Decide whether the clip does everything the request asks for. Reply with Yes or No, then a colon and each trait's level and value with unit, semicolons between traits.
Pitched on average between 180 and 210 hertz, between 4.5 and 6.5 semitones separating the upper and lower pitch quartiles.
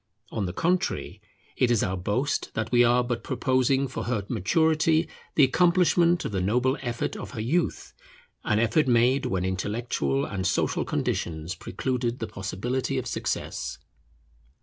No: low, 120 Hz; average, 4.9 semitones